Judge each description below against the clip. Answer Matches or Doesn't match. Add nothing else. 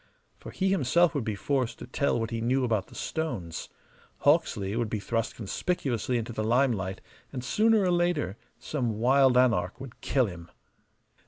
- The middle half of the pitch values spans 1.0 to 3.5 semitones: Doesn't match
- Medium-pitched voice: Doesn't match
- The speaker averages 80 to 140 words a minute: Doesn't match